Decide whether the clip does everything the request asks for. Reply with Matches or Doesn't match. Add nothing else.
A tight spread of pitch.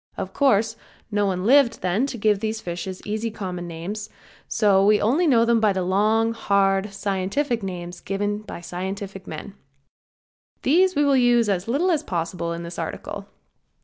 Doesn't match